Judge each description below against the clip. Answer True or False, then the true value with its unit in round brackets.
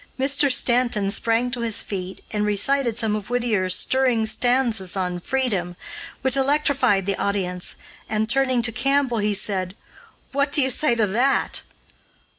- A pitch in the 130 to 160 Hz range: False (230 Hz)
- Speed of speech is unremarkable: True (150 wpm)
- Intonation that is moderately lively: True (4.6 semitones)